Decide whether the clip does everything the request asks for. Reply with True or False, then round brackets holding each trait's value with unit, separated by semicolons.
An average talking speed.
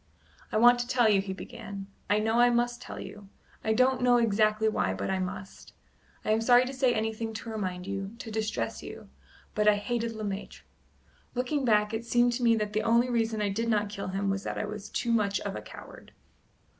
False (220 wpm)